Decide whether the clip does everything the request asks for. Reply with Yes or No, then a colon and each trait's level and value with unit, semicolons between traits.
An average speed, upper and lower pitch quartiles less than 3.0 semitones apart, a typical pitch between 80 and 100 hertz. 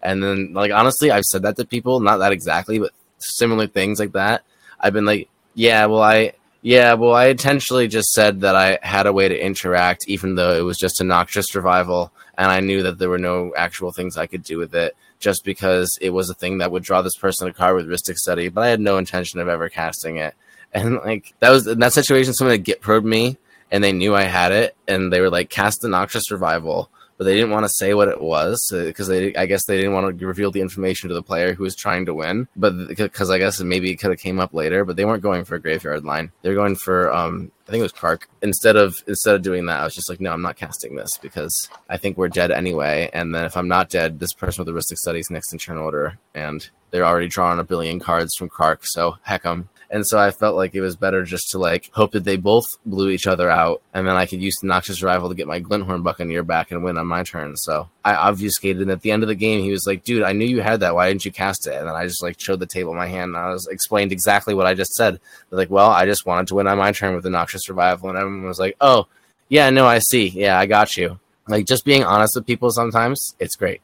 No: fast, 270 wpm; narrow, 2.4 semitones; very low, 95 Hz